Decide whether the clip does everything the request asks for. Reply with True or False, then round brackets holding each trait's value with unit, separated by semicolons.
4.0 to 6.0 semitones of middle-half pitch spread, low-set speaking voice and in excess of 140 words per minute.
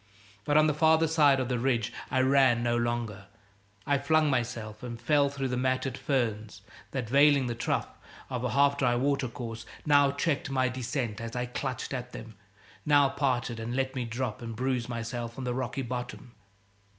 False (2.7 semitones; 130 Hz; 185 wpm)